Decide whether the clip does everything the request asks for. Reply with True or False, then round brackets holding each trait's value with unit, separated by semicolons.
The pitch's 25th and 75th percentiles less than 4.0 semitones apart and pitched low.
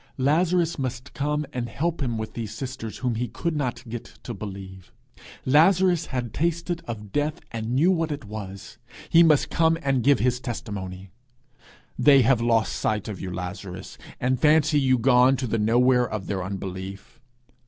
False (5.6 semitones; 125 Hz)